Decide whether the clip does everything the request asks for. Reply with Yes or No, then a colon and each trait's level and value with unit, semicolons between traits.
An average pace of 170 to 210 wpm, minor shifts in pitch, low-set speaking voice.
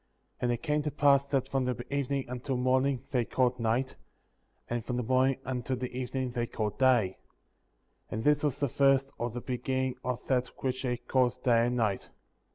Yes: average, 190 wpm; narrow, 1.8 semitones; low, 125 Hz